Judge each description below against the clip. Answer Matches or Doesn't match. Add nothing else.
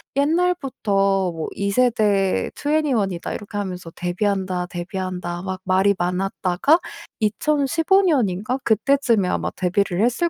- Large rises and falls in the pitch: Matches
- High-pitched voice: Matches